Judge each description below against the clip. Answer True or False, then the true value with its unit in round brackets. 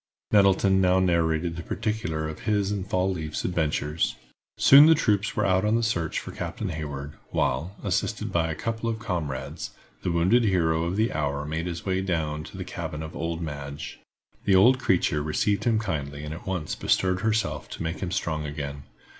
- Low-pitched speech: True (85 Hz)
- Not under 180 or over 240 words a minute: True (190 wpm)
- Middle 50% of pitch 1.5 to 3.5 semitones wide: False (4.3 semitones)